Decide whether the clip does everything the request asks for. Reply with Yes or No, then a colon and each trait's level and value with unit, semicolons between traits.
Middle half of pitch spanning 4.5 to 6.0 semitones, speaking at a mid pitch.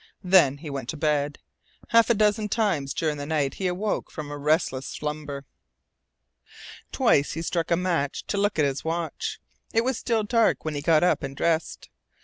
Yes: wide, 5.5 semitones; medium, 160 Hz